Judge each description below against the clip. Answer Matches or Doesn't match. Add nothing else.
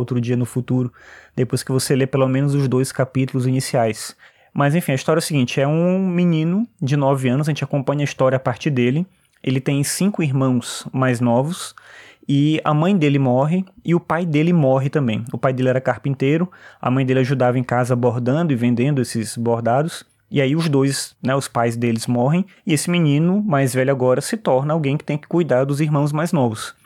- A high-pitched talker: Doesn't match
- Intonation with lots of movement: Doesn't match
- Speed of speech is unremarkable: Doesn't match